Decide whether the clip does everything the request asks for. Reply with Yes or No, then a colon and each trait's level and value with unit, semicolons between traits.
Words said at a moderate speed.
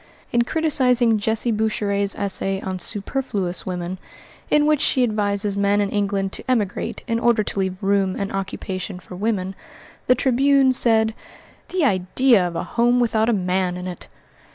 Yes: average, 160 wpm